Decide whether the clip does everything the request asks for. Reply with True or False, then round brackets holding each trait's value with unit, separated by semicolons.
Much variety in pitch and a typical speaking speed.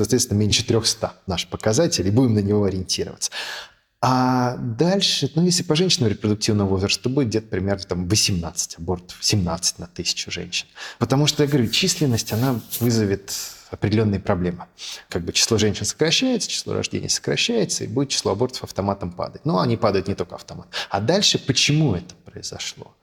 False (5.8 semitones; 165 wpm)